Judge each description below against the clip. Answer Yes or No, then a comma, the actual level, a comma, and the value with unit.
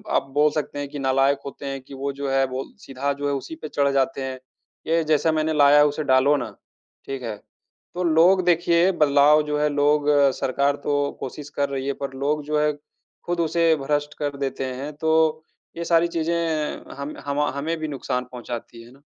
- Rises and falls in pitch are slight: Yes, narrow, 2.3 semitones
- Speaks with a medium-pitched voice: Yes, medium, 145 Hz